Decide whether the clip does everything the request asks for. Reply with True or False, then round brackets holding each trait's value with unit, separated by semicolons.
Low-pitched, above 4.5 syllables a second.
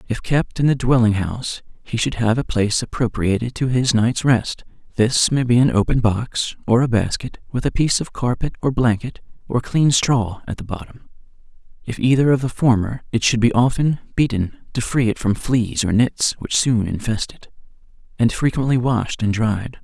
True (120 Hz; 5.0 syllables/s)